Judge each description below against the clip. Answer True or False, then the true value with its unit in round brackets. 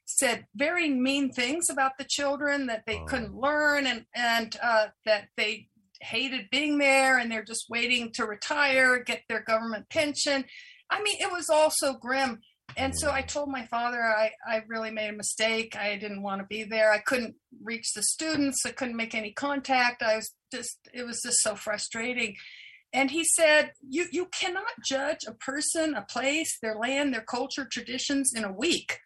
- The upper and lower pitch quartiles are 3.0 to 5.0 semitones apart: True (4.3 semitones)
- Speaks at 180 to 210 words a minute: True (190 wpm)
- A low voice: False (250 Hz)